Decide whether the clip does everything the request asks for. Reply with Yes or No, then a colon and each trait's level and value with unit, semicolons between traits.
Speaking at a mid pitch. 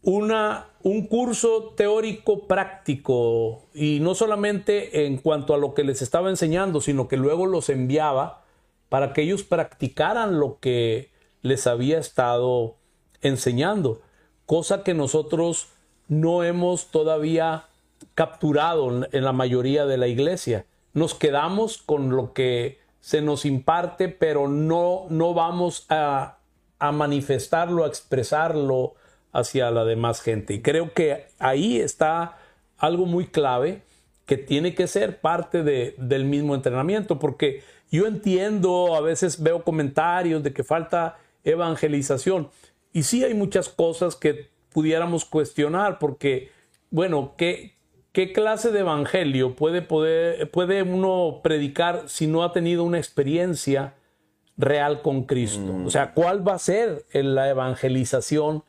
Yes: medium, 155 Hz